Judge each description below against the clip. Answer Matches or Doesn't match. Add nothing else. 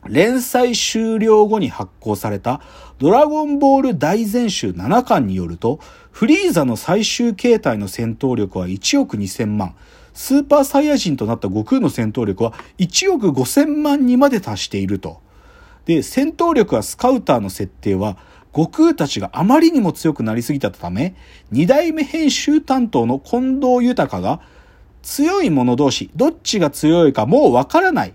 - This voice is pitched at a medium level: Matches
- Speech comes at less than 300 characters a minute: Matches